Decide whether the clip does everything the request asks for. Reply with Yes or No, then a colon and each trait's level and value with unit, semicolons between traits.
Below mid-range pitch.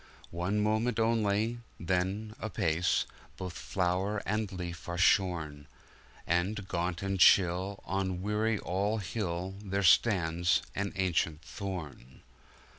Yes: very low, 95 Hz